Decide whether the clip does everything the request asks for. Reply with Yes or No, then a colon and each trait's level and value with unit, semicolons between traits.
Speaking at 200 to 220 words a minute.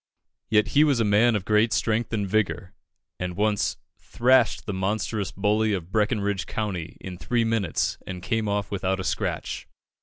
No: average, 170 wpm